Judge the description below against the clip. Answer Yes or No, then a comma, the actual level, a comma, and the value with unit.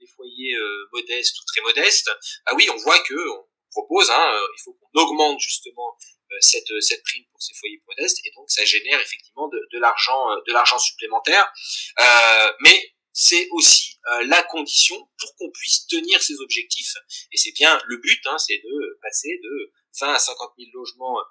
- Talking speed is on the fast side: No, average, 190 wpm